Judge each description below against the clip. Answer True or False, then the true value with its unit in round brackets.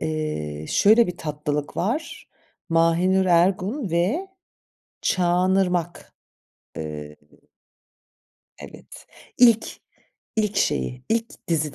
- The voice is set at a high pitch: False (175 Hz)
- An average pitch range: True (4.8 semitones)